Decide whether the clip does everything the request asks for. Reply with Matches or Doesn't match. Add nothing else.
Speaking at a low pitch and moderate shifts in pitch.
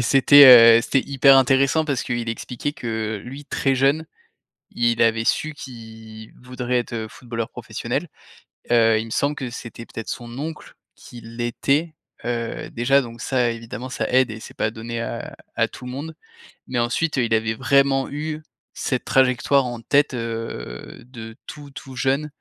Matches